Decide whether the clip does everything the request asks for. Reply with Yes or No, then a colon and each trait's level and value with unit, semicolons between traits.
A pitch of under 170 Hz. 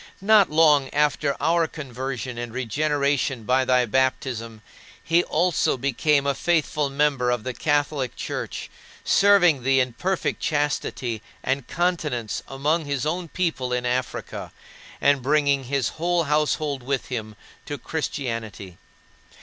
Yes: medium, 140 Hz